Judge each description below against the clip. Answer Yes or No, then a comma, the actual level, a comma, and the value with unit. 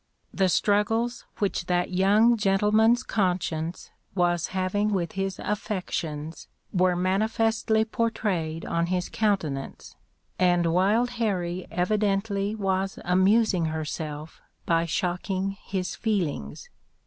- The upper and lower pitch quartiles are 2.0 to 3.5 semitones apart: Yes, average, 3.2 semitones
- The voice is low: No, high, 190 Hz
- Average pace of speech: No, slow, 100 wpm